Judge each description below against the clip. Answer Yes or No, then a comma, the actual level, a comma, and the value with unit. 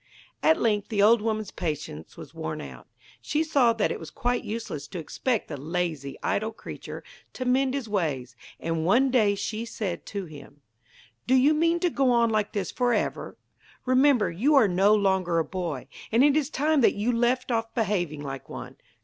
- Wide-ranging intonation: Yes, wide, 6.3 semitones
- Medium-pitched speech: No, high, 215 Hz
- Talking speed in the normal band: Yes, average, 190 wpm